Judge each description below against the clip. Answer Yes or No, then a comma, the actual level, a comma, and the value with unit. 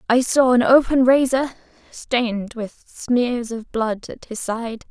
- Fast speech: No, average, 160 wpm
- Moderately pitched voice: No, high, 240 Hz